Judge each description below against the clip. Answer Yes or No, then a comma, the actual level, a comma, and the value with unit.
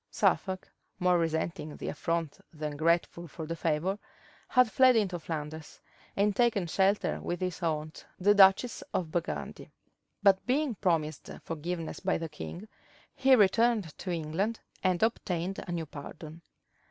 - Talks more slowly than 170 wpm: Yes, average, 140 wpm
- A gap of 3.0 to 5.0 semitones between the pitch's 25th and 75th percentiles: Yes, average, 3.9 semitones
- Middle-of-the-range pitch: Yes, medium, 175 Hz